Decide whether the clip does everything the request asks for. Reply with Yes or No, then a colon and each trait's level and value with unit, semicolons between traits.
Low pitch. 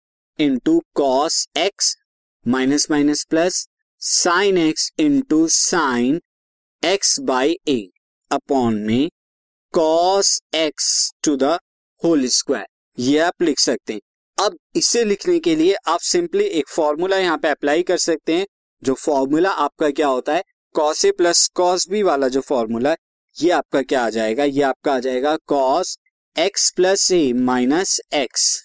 No: medium, 180 Hz